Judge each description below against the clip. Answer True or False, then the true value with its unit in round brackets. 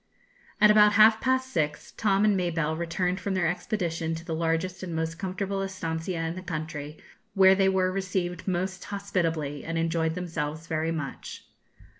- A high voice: False (175 Hz)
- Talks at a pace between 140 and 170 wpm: True (165 wpm)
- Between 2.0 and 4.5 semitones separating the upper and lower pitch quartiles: True (2.9 semitones)